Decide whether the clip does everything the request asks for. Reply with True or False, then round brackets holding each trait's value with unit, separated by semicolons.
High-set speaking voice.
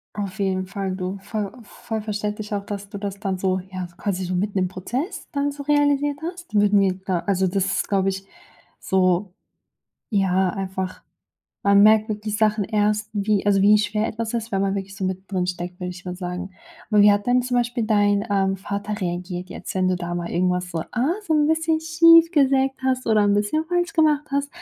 True (205 Hz)